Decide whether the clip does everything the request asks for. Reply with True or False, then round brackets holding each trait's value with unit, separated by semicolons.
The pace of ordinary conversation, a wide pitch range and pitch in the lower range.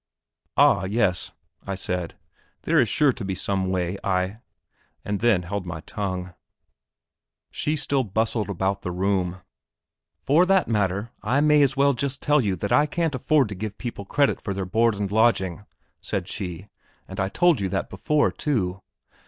True (170 wpm; 5.9 semitones; 100 Hz)